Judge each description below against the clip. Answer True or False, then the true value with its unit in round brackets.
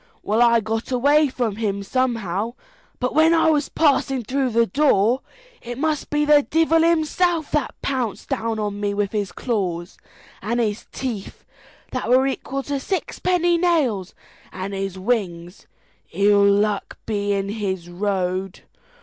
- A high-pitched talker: True (230 Hz)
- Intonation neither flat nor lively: False (5.9 semitones)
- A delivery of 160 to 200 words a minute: False (150 wpm)